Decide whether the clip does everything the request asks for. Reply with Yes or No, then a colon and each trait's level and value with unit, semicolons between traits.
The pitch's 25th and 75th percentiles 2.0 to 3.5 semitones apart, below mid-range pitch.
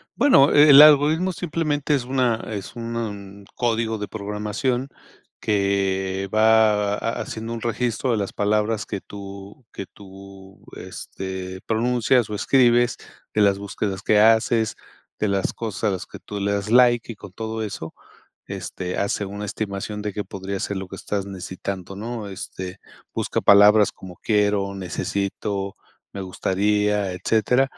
Yes: average, 2.8 semitones; low, 105 Hz